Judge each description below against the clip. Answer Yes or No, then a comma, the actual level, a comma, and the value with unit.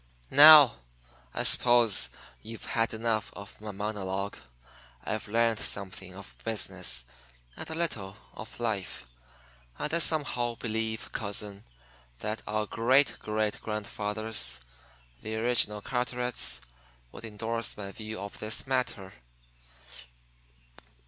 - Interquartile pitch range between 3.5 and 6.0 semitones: No, narrow, 2.4 semitones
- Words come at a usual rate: No, slow, 110 wpm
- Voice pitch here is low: Yes, low, 110 Hz